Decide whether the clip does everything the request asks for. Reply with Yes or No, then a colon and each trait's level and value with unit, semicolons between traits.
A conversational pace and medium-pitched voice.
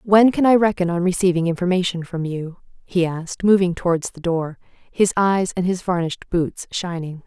Yes: average, 180 wpm; medium, 180 Hz